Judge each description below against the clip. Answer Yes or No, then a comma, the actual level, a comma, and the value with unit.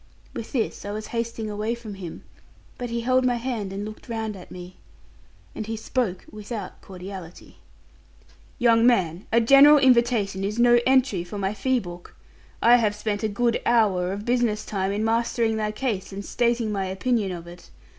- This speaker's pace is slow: No, average, 180 wpm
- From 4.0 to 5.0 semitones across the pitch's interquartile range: No, average, 3.3 semitones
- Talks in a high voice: Yes, high, 215 Hz